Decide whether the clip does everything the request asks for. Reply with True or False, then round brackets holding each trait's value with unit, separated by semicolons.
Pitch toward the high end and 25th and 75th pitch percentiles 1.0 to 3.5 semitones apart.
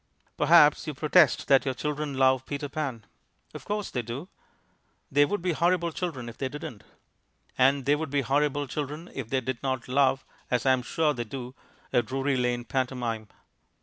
False (135 Hz; 2.7 semitones)